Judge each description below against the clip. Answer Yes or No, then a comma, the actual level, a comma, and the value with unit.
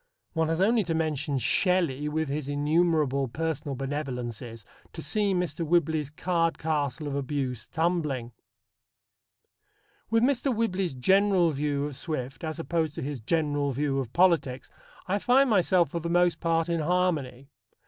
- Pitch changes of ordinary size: Yes, average, 4.0 semitones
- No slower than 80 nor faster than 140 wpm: No, average, 150 wpm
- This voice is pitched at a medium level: Yes, medium, 155 Hz